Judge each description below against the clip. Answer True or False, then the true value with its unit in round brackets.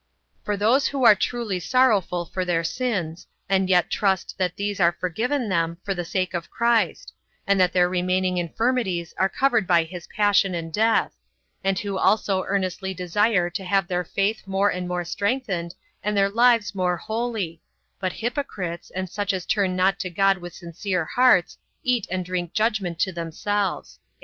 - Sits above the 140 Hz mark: True (190 Hz)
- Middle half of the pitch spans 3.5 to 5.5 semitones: False (2.8 semitones)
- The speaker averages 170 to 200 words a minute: True (175 wpm)